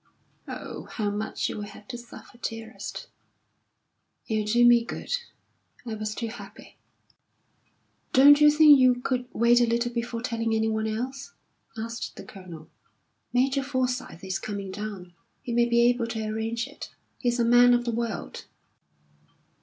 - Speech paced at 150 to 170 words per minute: Yes, average, 155 wpm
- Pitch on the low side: No, high, 235 Hz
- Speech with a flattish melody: Yes, narrow, 2.1 semitones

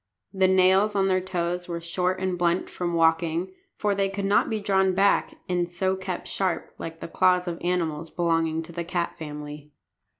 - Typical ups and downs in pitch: No, narrow, 2.1 semitones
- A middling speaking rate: Yes, average, 190 wpm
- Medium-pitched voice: Yes, medium, 180 Hz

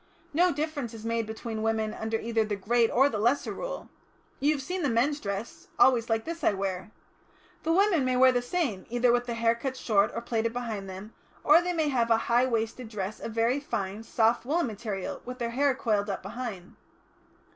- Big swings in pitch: No, average, 3.3 semitones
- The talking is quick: Yes, fast, 210 wpm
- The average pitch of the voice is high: Yes, high, 235 Hz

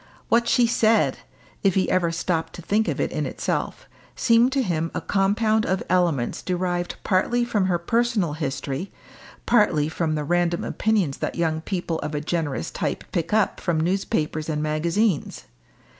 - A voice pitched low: No, medium, 175 Hz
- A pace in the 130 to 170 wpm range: Yes, average, 165 wpm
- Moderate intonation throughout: Yes, average, 5.0 semitones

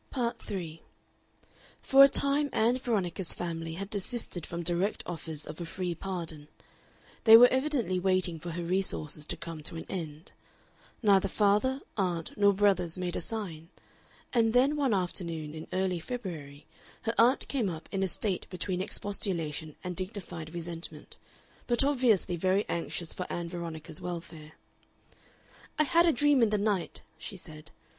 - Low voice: No, medium, 185 Hz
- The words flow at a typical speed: Yes, average, 155 wpm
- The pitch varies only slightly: No, average, 4.7 semitones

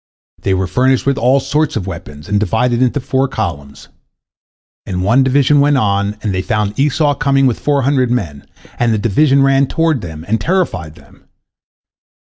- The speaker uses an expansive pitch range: Yes, wide, 5.7 semitones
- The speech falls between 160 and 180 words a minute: Yes, average, 175 wpm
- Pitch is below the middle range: Yes, low, 125 Hz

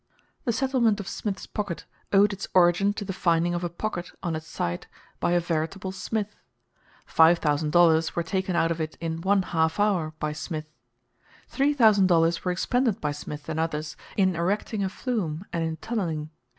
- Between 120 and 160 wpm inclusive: No, average, 185 wpm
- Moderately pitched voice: Yes, medium, 175 Hz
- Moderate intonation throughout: Yes, average, 3.8 semitones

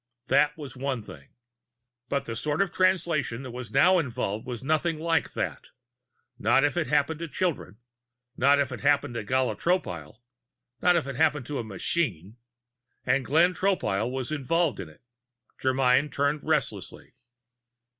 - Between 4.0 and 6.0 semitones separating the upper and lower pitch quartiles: Yes, average, 4.3 semitones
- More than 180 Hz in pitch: No, medium, 140 Hz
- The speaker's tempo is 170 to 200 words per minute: No, average, 155 wpm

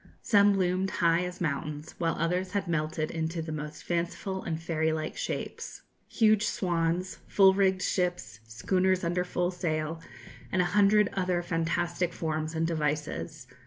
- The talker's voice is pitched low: No, medium, 175 Hz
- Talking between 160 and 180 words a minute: No, average, 150 wpm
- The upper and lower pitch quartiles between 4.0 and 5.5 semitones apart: No, average, 2.7 semitones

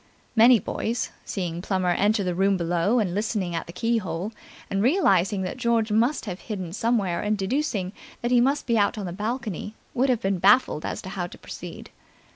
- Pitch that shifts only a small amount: No, average, 4.1 semitones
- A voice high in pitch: Yes, high, 205 Hz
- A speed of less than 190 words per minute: No, average, 195 wpm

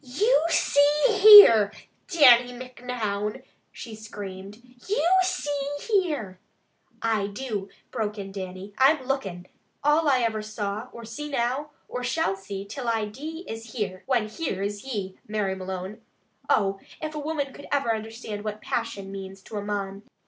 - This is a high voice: Yes, high, 225 Hz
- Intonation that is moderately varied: No, wide, 5.7 semitones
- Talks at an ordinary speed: Yes, average, 155 wpm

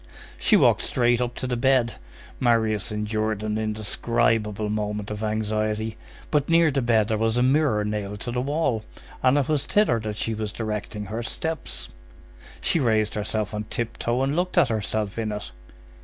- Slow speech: No, average, 175 wpm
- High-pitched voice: No, low, 110 Hz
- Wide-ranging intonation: No, average, 2.7 semitones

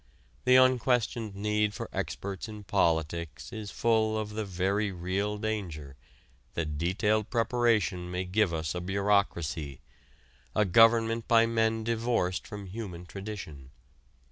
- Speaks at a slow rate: Yes, slow, 125 wpm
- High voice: No, low, 105 Hz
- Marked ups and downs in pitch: No, average, 3.9 semitones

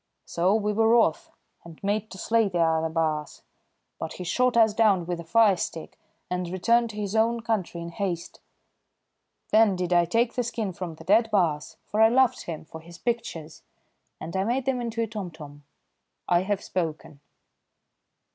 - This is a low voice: No, high, 190 Hz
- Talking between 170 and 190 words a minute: Yes, average, 180 wpm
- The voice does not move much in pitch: No, average, 5.0 semitones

